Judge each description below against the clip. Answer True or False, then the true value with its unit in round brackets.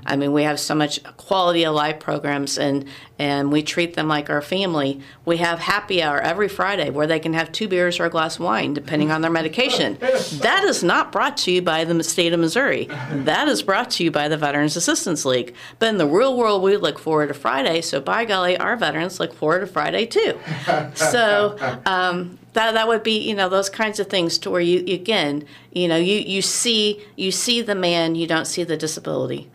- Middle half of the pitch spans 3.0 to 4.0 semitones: False (4.6 semitones)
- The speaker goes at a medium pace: False (225 wpm)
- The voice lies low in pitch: False (170 Hz)